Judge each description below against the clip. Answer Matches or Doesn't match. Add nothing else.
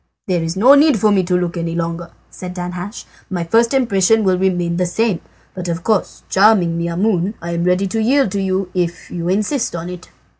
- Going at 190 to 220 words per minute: Matches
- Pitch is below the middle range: Doesn't match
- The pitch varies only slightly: Doesn't match